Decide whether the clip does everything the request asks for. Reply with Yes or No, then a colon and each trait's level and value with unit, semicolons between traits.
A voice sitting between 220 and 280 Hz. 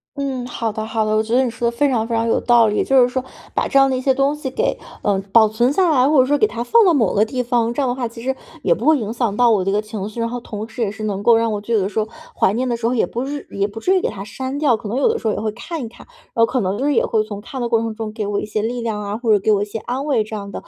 Yes: high, 230 Hz